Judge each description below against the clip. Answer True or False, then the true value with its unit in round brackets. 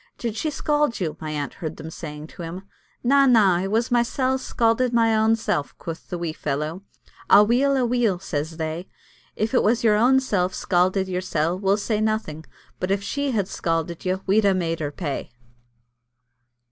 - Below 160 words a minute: False (180 wpm)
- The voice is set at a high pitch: True (195 Hz)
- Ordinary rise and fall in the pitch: False (5.8 semitones)